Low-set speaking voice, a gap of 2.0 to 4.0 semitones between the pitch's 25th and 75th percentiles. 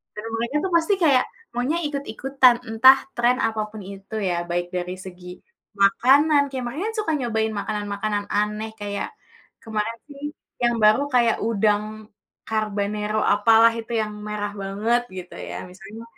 No: high, 220 Hz; average, 3.0 semitones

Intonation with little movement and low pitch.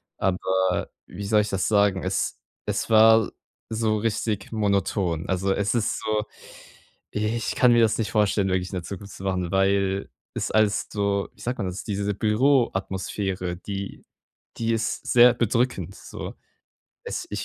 Yes: narrow, 2.3 semitones; low, 100 Hz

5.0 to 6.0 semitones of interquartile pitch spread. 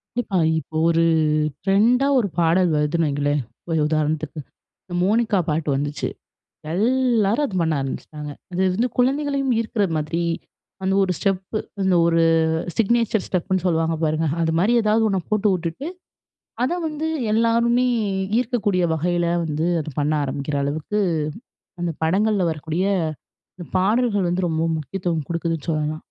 Yes: wide, 5.5 semitones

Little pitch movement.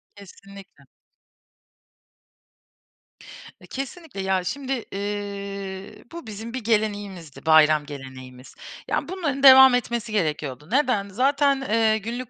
No: average, 5.1 semitones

